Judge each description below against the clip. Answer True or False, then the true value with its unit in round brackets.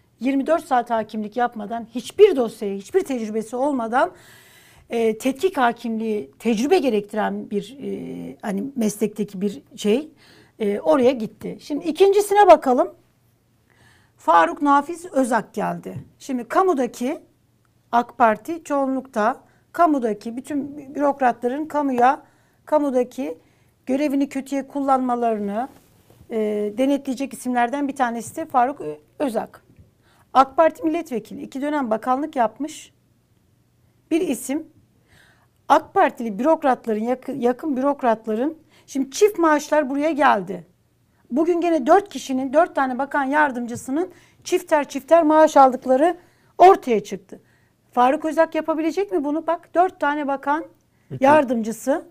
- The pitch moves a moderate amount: True (4.8 semitones)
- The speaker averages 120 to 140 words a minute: False (110 wpm)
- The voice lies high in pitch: True (270 Hz)